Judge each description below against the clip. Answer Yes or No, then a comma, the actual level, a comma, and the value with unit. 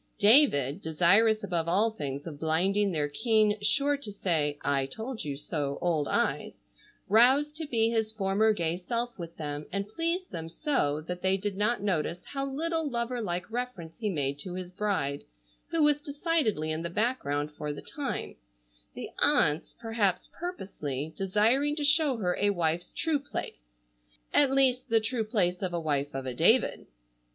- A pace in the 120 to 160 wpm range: No, average, 170 wpm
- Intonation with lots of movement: Yes, wide, 7.4 semitones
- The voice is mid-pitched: No, high, 195 Hz